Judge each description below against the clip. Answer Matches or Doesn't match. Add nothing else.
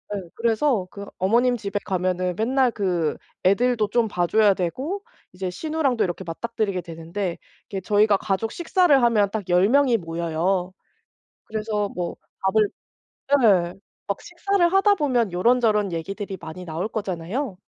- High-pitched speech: Matches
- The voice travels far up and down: Doesn't match